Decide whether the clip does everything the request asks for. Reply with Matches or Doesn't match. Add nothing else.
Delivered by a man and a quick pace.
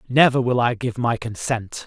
Doesn't match